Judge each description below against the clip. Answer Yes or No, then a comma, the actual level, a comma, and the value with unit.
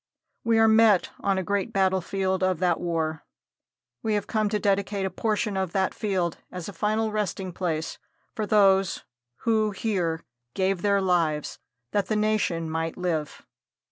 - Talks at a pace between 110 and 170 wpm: Yes, average, 160 wpm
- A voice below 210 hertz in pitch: Yes, high, 190 Hz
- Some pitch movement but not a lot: Yes, average, 3.1 semitones